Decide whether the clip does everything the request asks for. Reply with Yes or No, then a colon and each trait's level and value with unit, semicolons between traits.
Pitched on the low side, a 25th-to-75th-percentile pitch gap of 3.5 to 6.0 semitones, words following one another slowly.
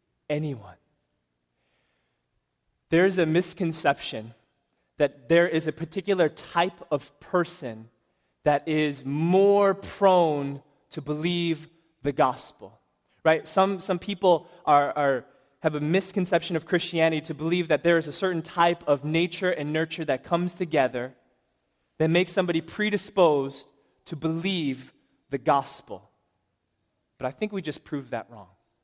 No: medium, 160 Hz; average, 4.0 semitones; slow, 130 wpm